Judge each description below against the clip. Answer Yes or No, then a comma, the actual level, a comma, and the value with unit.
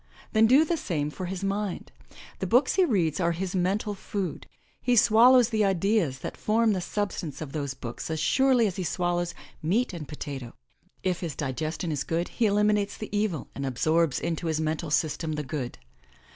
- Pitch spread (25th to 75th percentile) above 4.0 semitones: Yes, average, 5.2 semitones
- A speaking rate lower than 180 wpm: No, average, 185 wpm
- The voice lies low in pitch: No, medium, 180 Hz